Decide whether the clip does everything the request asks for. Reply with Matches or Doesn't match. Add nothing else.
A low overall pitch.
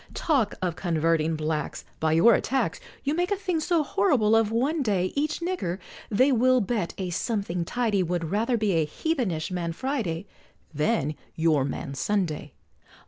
Doesn't match